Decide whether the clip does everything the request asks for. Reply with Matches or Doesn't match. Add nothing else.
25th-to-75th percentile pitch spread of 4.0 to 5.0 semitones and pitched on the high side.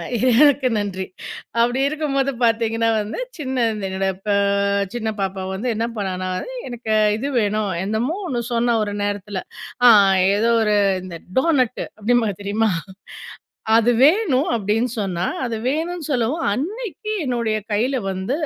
Matches